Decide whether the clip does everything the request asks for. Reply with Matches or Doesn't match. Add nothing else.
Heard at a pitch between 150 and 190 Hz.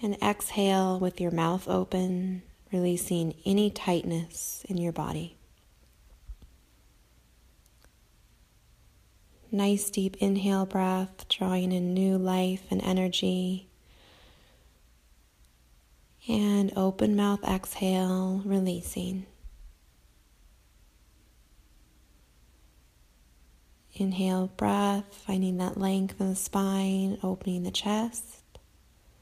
Matches